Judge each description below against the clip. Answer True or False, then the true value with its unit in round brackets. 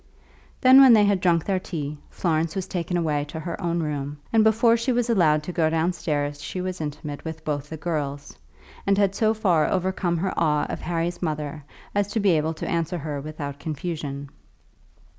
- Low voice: False (165 Hz)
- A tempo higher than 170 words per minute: True (195 wpm)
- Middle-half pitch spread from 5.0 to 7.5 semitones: False (3.9 semitones)